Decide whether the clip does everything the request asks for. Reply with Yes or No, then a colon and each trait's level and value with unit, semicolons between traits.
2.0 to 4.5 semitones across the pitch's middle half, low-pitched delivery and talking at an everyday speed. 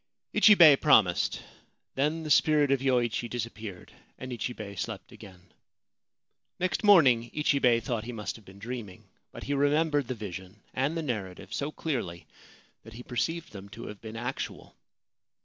No: average, 5.3 semitones; low, 120 Hz; average, 155 wpm